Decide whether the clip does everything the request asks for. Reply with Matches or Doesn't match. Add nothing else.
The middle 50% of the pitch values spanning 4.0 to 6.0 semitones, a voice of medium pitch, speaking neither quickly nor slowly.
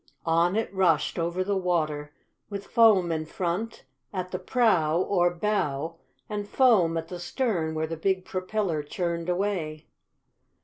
Doesn't match